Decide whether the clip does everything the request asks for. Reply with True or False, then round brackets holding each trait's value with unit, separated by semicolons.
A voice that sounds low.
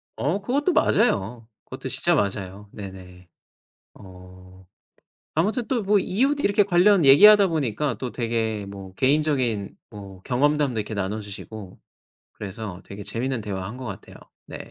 True (115 Hz)